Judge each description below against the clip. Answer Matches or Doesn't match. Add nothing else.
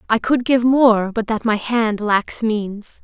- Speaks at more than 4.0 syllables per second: Doesn't match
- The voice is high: Matches